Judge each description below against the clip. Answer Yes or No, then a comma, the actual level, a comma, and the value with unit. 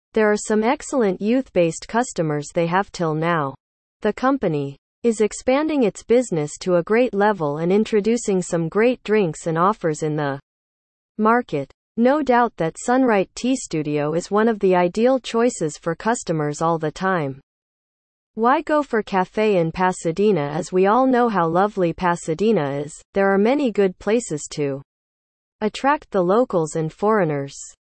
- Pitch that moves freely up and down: Yes, wide, 6.1 semitones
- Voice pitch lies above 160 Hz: Yes, high, 190 Hz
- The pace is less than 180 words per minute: Yes, average, 155 wpm